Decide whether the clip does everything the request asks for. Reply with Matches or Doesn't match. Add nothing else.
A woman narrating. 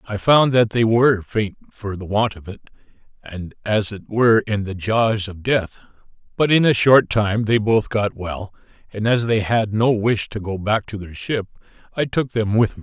Doesn't match